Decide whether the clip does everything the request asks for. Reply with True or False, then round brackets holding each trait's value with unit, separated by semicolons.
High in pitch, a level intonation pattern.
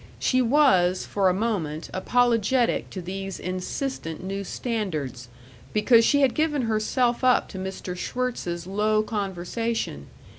False (210 Hz; 4.9 semitones)